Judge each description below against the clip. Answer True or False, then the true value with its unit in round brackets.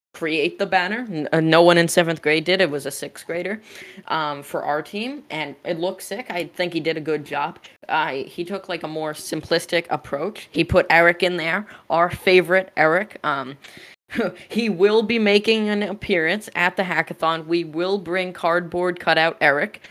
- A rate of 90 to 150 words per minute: False (185 wpm)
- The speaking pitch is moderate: True (175 Hz)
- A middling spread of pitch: True (3.1 semitones)